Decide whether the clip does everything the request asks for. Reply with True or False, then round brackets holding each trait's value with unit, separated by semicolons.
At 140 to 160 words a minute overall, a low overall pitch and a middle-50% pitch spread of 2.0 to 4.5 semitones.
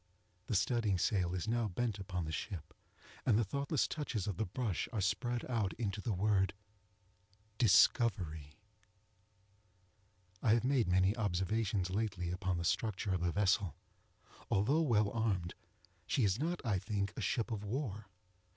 True (150 wpm; 105 Hz; 3.8 semitones)